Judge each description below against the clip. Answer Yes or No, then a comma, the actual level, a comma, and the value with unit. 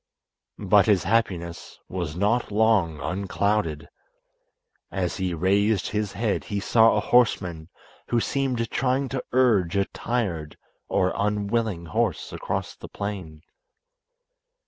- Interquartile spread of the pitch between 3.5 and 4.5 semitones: Yes, average, 4.0 semitones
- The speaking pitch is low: Yes, low, 100 Hz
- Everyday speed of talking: No, slow, 120 wpm